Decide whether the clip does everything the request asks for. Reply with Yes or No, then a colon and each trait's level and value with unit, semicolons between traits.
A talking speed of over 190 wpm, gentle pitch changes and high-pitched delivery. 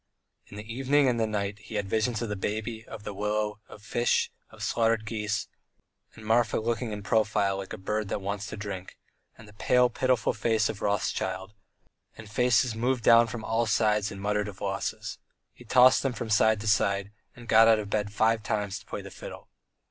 No: average, 200 wpm; narrow, 1.8 semitones; low, 110 Hz